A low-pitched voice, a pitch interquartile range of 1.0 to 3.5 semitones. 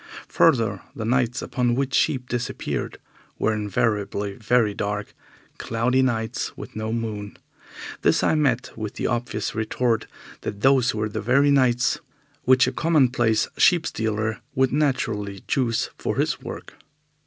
Yes: low, 115 Hz; average, 3.0 semitones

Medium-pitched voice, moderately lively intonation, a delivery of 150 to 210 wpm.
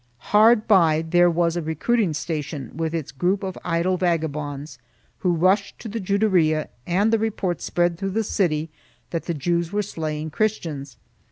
Yes: medium, 175 Hz; average, 4.0 semitones; average, 165 wpm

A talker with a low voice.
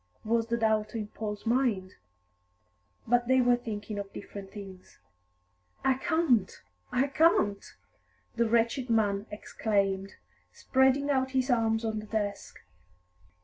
No: high, 225 Hz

